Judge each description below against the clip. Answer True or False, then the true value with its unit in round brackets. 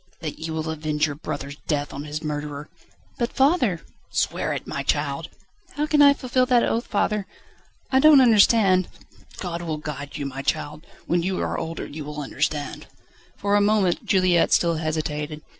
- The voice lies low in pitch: False (160 Hz)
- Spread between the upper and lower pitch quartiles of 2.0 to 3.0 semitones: False (5.6 semitones)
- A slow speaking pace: False (180 wpm)